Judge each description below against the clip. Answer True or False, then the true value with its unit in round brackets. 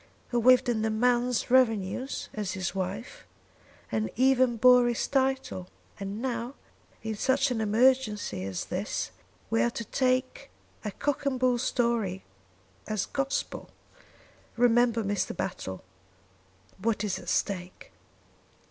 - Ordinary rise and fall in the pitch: True (3.9 semitones)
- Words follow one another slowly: True (130 wpm)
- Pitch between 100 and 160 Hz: False (235 Hz)